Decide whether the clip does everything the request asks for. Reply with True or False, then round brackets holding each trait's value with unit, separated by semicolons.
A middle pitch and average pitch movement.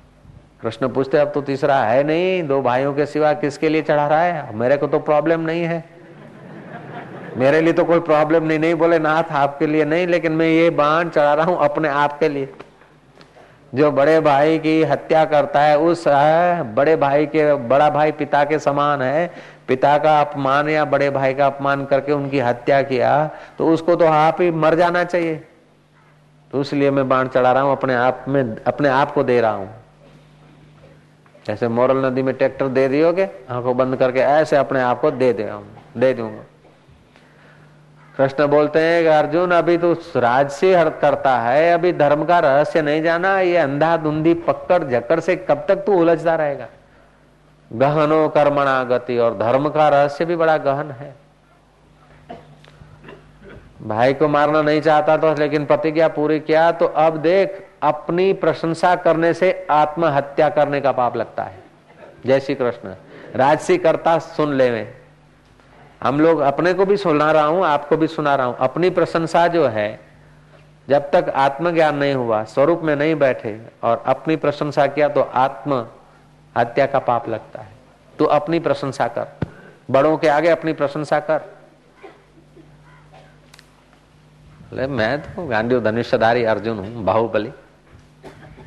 True (150 Hz; 3.0 semitones)